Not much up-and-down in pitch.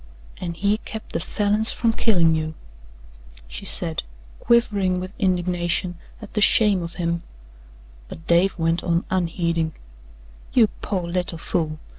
No: average, 3.3 semitones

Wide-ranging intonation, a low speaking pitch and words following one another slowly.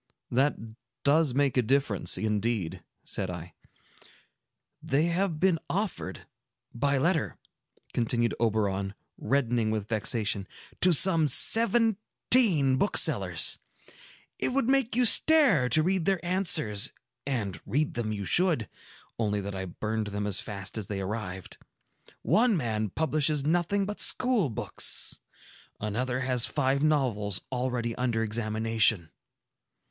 Yes: wide, 7.5 semitones; low, 125 Hz; slow, 120 wpm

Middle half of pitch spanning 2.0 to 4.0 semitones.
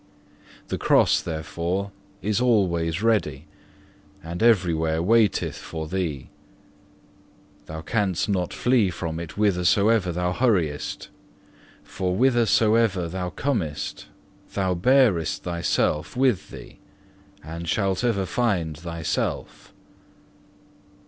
No: average, 4.7 semitones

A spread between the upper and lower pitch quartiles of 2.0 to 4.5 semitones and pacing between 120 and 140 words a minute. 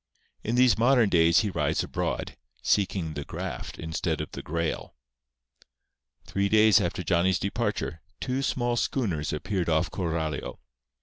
No: average, 4.9 semitones; slow, 135 wpm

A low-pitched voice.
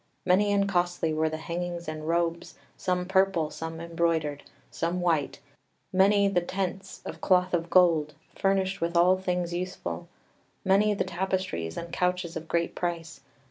No: medium, 175 Hz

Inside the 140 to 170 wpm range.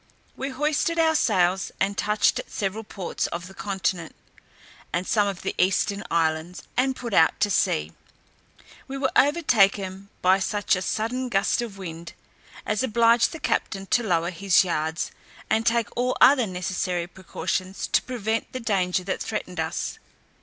Yes: average, 160 wpm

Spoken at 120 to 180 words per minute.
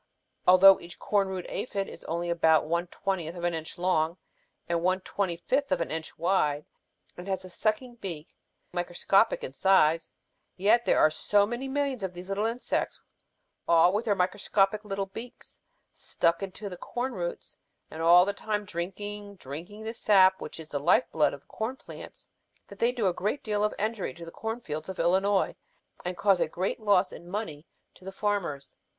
No: average, 195 wpm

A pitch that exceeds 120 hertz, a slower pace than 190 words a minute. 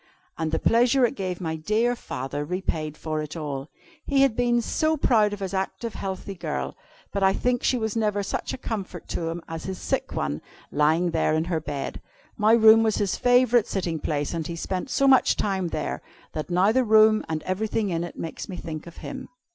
No: high, 190 Hz; fast, 205 wpm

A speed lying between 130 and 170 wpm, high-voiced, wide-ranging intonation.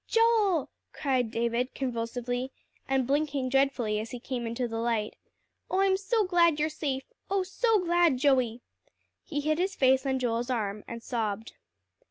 Yes: average, 160 wpm; very high, 265 Hz; wide, 5.9 semitones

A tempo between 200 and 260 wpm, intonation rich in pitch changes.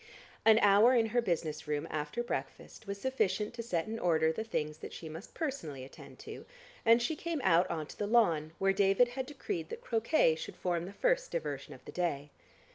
Yes: fast, 205 wpm; wide, 6.8 semitones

